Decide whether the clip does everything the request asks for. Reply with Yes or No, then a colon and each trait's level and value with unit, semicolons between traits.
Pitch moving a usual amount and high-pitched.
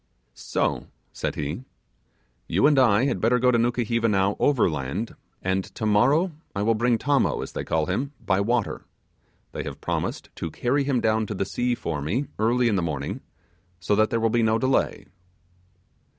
No: average, 4.2 semitones; low, 115 Hz